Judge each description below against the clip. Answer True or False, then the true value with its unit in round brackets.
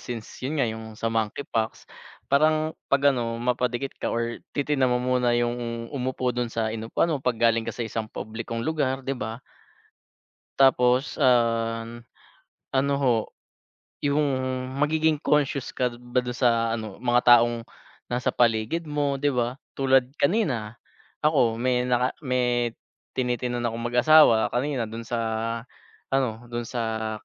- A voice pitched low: True (125 Hz)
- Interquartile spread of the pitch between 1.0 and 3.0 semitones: True (2.7 semitones)